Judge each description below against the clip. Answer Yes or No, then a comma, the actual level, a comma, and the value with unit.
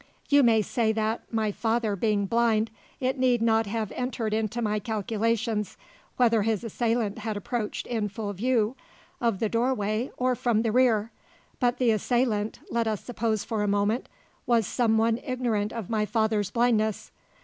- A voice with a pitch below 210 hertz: No, high, 225 Hz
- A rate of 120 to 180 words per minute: Yes, average, 165 wpm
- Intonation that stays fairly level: Yes, narrow, 1.9 semitones